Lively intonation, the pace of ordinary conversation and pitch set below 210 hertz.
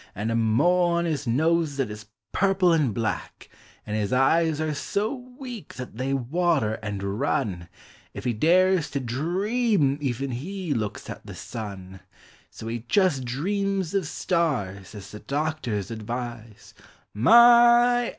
Yes: wide, 8.1 semitones; average, 150 wpm; medium, 140 Hz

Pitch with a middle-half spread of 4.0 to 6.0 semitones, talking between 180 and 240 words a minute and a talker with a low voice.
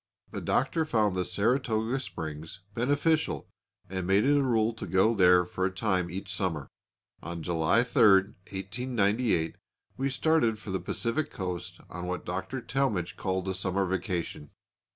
No: average, 4.6 semitones; average, 150 wpm; low, 100 Hz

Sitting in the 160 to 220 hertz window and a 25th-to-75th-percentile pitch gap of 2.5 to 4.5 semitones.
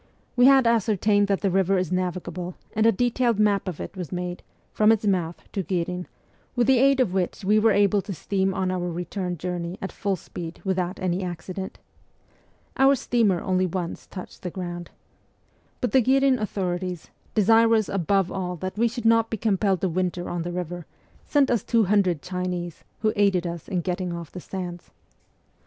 Yes: high, 190 Hz; average, 3.2 semitones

